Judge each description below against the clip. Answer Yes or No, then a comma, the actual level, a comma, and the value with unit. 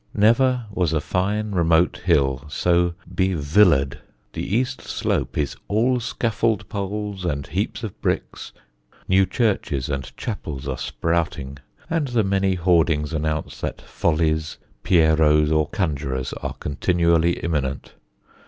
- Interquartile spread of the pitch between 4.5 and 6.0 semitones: Yes, average, 5.2 semitones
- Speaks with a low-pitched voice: Yes, very low, 85 Hz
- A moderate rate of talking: No, slow, 125 wpm